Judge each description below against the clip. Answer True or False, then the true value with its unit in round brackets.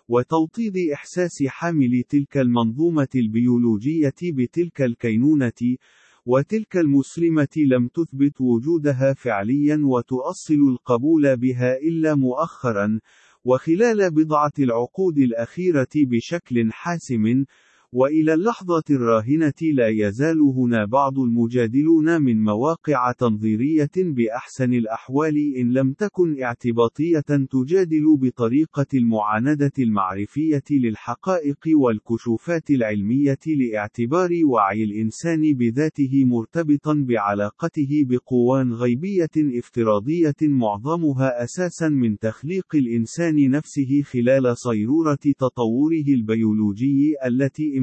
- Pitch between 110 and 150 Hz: True (135 Hz)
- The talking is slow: False (85 wpm)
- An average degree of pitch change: True (4.5 semitones)